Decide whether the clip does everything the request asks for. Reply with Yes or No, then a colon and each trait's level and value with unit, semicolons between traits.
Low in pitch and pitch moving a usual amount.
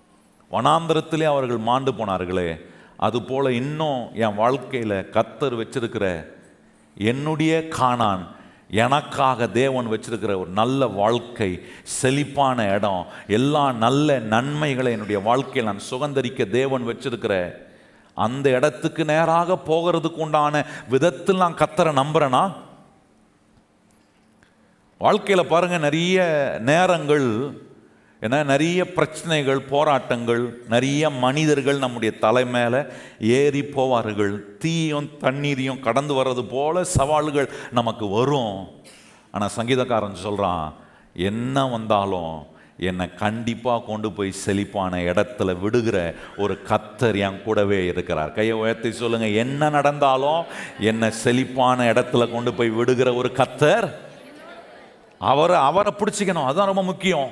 Yes: low, 125 Hz; average, 5.0 semitones